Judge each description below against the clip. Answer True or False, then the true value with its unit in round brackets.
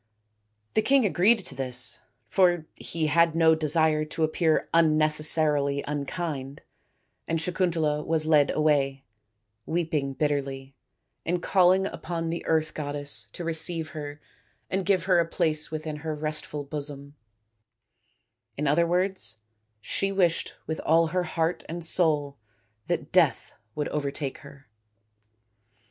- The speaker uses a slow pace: True (125 wpm)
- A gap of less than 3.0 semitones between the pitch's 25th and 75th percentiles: True (2.5 semitones)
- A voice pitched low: False (155 Hz)